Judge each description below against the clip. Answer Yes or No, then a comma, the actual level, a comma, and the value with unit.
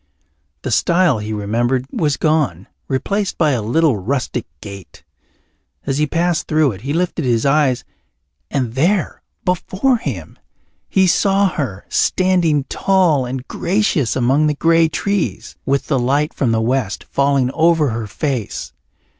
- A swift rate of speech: No, average, 145 wpm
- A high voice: No, medium, 140 Hz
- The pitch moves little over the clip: No, average, 5.3 semitones